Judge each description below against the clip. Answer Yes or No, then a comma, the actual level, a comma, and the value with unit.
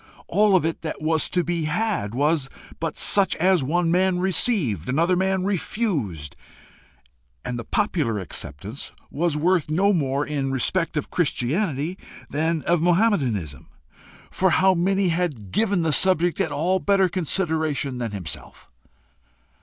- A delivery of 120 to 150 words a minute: Yes, average, 140 wpm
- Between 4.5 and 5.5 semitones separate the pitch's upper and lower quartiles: Yes, average, 5.1 semitones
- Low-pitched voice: No, medium, 165 Hz